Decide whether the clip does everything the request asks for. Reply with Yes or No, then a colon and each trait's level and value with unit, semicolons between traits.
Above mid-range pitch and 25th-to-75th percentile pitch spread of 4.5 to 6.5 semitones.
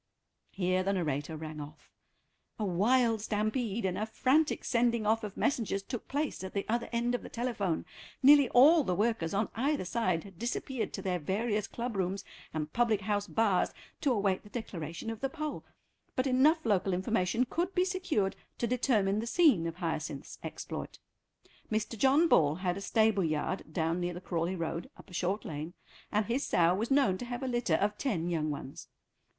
Yes: high, 210 Hz; average, 5.2 semitones